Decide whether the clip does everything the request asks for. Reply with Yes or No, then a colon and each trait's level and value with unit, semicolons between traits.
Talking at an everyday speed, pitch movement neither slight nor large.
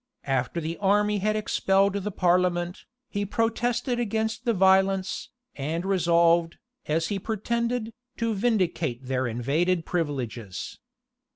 No: slow, 115 wpm; average, 4.5 semitones